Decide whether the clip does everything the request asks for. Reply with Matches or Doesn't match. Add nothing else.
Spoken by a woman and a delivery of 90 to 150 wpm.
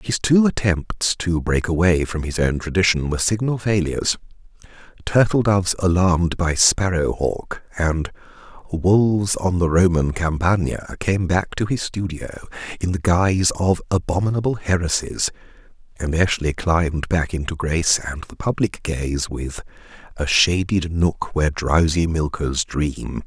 Doesn't match